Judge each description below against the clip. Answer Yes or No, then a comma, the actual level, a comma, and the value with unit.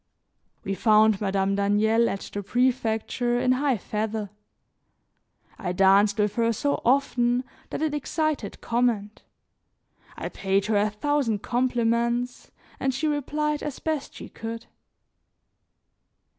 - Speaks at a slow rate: Yes, slow, 120 wpm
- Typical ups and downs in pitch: Yes, average, 3.9 semitones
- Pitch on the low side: No, high, 230 Hz